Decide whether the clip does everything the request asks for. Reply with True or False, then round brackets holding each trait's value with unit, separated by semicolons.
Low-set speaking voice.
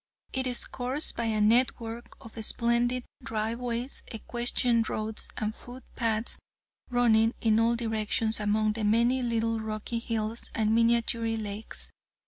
False (230 Hz)